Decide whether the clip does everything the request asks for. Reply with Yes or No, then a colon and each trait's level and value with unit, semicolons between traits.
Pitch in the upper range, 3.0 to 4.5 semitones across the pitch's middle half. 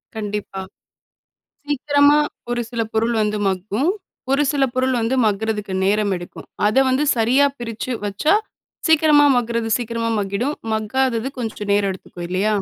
Yes: high, 225 Hz; average, 4.0 semitones